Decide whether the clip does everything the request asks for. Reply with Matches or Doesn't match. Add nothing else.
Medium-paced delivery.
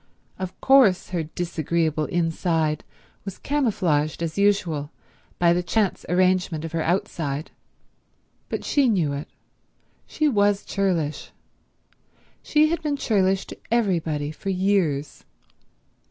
Doesn't match